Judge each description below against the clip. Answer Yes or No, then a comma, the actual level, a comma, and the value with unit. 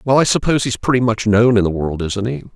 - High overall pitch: No, low, 110 Hz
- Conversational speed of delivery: No, fast, 280 wpm